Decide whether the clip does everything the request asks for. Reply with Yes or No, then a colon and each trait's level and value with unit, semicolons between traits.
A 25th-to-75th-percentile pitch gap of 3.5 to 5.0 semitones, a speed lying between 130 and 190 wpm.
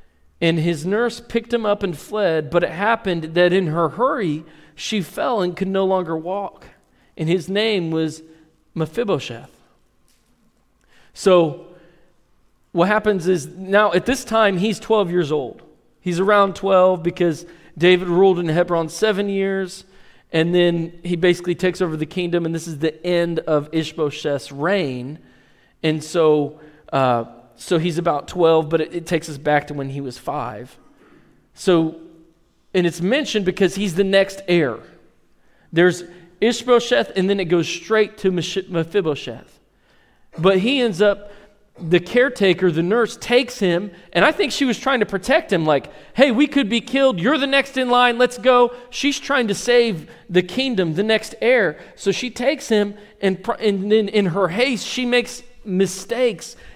Yes: average, 4.5 semitones; average, 165 wpm